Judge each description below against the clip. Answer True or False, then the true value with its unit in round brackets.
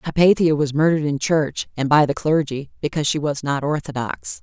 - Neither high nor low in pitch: True (150 Hz)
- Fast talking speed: False (190 wpm)